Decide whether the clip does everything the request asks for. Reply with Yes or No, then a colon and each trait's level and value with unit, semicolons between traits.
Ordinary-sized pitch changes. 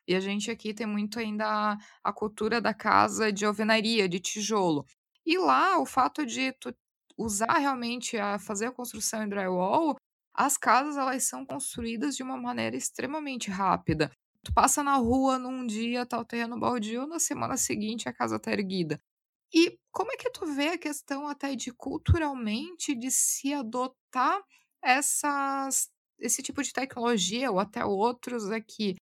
Yes: average, 4.5 semitones